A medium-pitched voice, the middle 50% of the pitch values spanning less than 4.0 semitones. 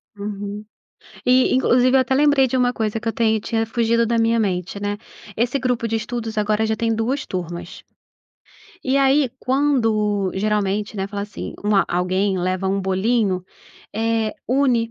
No: high, 220 Hz; average, 3.4 semitones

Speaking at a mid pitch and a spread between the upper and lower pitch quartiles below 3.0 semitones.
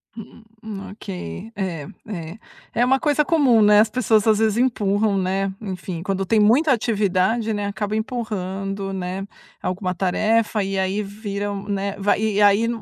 No: high, 205 Hz; narrow, 2.4 semitones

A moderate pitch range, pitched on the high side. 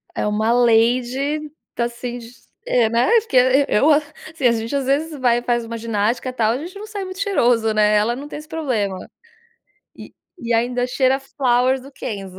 Yes: average, 3.6 semitones; high, 245 Hz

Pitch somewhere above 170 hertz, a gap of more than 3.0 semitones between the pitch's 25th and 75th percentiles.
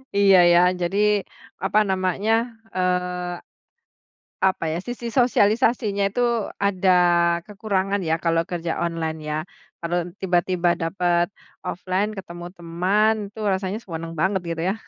No: medium, 185 Hz; narrow, 2.6 semitones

